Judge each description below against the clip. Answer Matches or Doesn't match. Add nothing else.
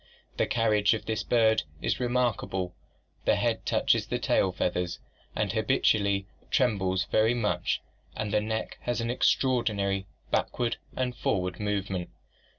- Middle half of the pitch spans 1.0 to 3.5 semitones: Matches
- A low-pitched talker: Matches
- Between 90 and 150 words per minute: Matches